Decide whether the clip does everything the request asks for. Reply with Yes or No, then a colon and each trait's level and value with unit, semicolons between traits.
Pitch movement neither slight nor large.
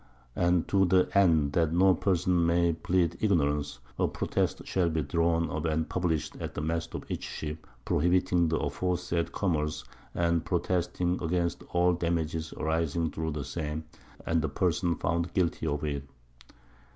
No: narrow, 2.1 semitones